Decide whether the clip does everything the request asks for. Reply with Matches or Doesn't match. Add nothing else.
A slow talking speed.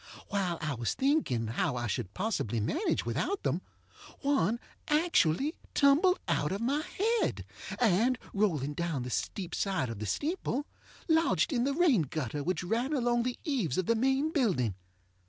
Doesn't match